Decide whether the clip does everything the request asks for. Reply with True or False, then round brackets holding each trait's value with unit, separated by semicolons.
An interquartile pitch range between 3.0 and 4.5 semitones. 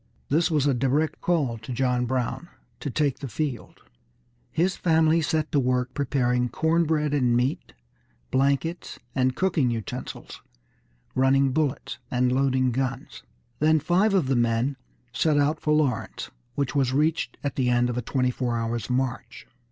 True (3.5 semitones)